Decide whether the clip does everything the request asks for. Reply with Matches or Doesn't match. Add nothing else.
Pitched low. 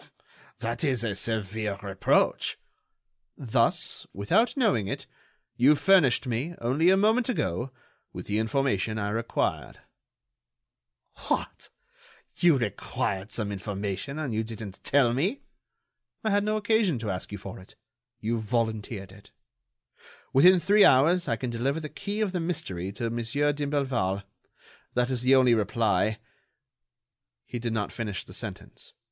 Matches